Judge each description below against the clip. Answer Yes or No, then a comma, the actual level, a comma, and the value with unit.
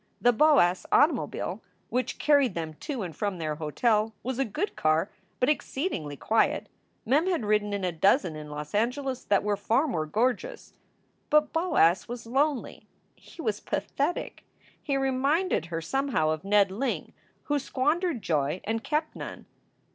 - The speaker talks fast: No, average, 155 wpm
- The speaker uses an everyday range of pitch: No, wide, 8.0 semitones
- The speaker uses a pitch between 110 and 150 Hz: No, high, 230 Hz